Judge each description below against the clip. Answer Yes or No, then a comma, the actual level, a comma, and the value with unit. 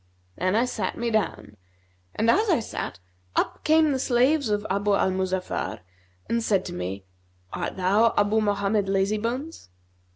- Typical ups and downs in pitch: Yes, average, 3.8 semitones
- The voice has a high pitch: Yes, high, 210 Hz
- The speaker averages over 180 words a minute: No, average, 155 wpm